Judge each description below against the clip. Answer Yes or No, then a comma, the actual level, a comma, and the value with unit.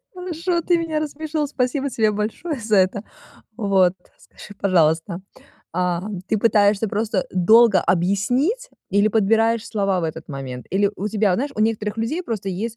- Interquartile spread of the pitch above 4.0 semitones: Yes, average, 4.6 semitones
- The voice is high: Yes, high, 215 Hz